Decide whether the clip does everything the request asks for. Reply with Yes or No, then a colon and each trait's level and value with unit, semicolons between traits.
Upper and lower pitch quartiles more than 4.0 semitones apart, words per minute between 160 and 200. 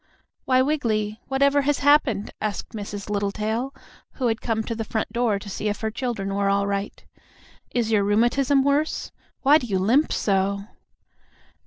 Yes: average, 4.7 semitones; average, 165 wpm